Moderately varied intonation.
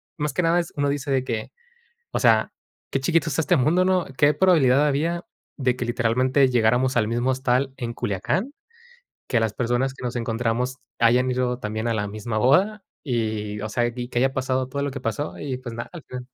Yes: average, 3.3 semitones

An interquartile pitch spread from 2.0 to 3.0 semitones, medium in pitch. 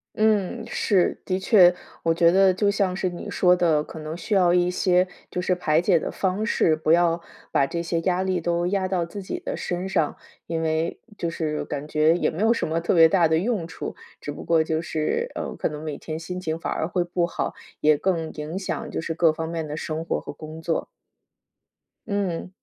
Yes: narrow, 2.5 semitones; medium, 170 Hz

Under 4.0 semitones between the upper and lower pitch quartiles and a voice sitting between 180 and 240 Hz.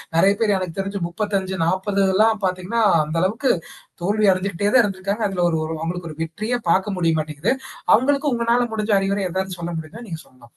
Yes: average, 3.6 semitones; high, 195 Hz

